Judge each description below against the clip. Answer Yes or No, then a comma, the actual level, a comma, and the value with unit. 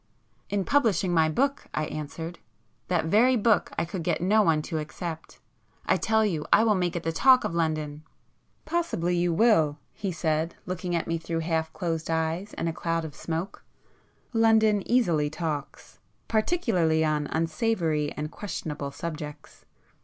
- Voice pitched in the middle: Yes, medium, 170 Hz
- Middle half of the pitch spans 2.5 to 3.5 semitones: No, average, 4.6 semitones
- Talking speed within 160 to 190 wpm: No, average, 150 wpm